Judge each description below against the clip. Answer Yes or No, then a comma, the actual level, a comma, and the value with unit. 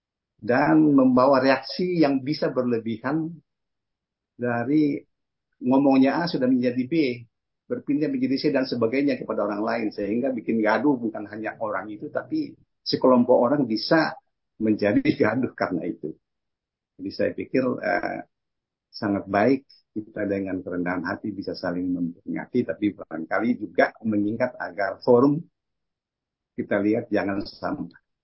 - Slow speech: No, average, 125 wpm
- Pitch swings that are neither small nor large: No, wide, 5.9 semitones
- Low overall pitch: Yes, low, 125 Hz